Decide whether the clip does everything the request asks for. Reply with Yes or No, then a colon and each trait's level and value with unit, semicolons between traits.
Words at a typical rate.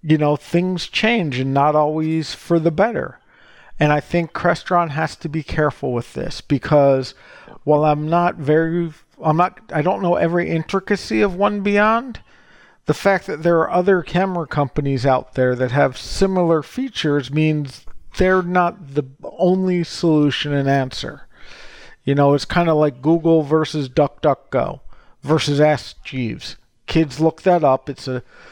Yes: average, 160 wpm